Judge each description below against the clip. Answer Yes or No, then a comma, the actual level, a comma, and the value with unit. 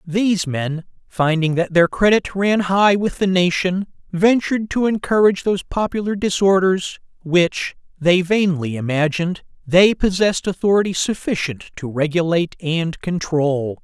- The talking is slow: Yes, slow, 125 wpm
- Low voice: No, medium, 180 Hz